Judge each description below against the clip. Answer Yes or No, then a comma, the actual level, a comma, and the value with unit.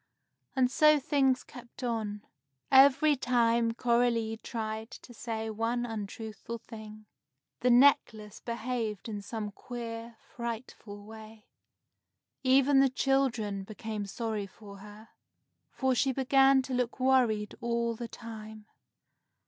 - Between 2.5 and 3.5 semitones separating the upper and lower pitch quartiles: Yes, average, 2.8 semitones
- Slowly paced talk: Yes, slow, 115 wpm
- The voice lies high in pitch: Yes, high, 230 Hz